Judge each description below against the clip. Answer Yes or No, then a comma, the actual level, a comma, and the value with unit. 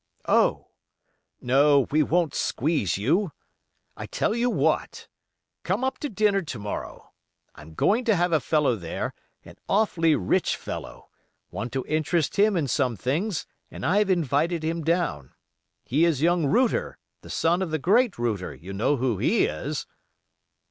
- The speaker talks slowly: No, average, 155 wpm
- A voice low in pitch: No, medium, 160 Hz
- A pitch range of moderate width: No, wide, 6.5 semitones